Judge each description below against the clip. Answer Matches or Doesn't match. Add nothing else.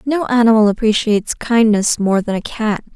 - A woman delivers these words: Matches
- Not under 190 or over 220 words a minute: Doesn't match